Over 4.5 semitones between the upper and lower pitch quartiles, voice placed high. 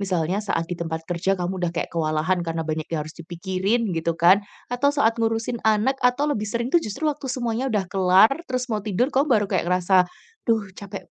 Yes: average, 5.3 semitones; high, 200 Hz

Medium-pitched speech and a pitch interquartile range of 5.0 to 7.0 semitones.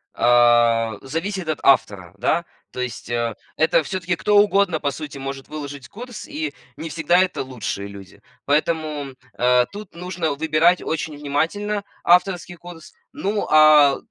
Yes: medium, 155 Hz; wide, 5.5 semitones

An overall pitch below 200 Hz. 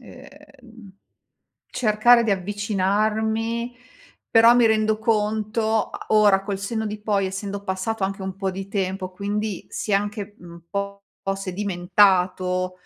No: high, 205 Hz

